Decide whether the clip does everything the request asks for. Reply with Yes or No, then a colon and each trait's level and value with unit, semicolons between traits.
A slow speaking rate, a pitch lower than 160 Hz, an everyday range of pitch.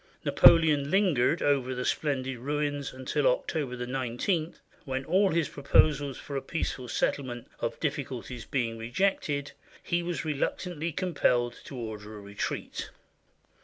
Yes: slow, 130 wpm; medium, 140 Hz; average, 4.3 semitones